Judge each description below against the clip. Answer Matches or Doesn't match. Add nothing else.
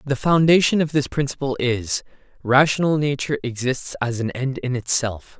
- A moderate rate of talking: Matches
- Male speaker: Matches